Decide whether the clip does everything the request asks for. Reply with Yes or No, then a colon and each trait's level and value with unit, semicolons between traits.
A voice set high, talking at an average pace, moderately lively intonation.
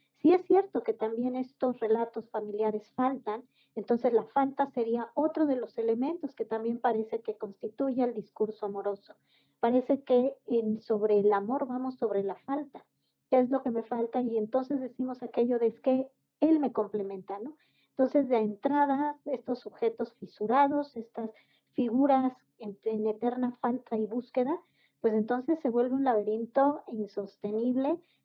Yes: high, 245 Hz; average, 155 wpm; average, 3.5 semitones